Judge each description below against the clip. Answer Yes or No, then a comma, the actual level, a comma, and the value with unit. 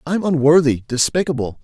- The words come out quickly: No, slow, 110 wpm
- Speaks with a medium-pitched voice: Yes, medium, 150 Hz